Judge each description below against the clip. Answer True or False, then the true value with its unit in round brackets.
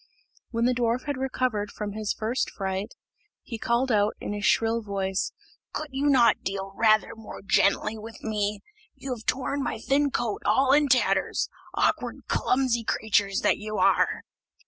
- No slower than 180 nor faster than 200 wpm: False (165 wpm)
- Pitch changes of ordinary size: True (3.6 semitones)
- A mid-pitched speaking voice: False (225 Hz)